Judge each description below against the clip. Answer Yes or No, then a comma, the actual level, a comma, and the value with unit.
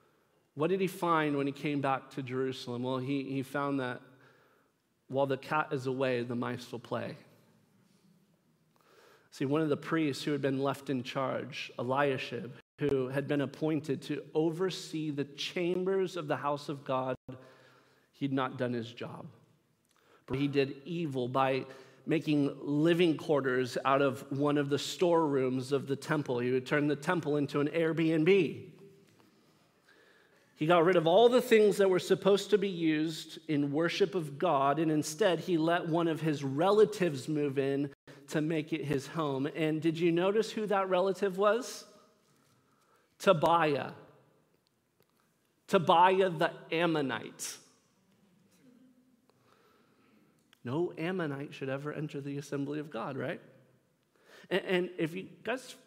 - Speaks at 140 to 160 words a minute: Yes, average, 145 wpm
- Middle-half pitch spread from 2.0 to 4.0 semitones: No, average, 4.7 semitones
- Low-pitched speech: No, medium, 155 Hz